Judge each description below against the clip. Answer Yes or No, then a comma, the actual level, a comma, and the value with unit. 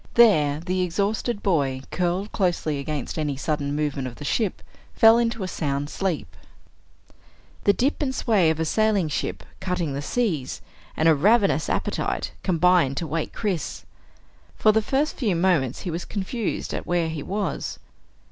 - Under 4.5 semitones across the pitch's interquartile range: No, wide, 5.6 semitones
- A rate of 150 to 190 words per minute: Yes, average, 160 wpm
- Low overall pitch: No, medium, 175 Hz